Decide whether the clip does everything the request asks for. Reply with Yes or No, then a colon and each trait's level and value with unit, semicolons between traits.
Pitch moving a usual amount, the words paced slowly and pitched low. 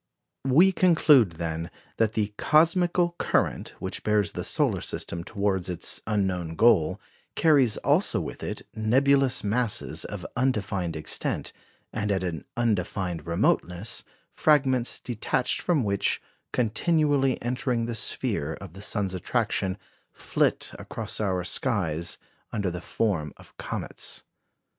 No: wide, 6.1 semitones; slow, 125 wpm; low, 105 Hz